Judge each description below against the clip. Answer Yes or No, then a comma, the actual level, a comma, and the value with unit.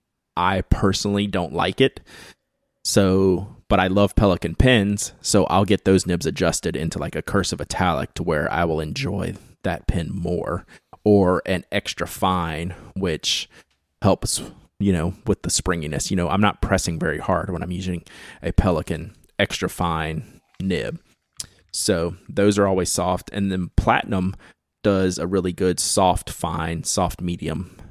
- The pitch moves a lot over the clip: No, narrow, 2.4 semitones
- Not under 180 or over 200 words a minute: No, average, 155 wpm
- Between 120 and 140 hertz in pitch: No, very low, 95 Hz